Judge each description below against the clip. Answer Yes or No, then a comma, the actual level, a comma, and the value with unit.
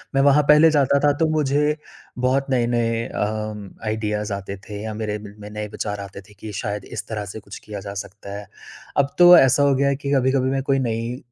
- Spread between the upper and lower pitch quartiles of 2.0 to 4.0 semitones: No, average, 4.7 semitones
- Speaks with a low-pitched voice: Yes, low, 115 Hz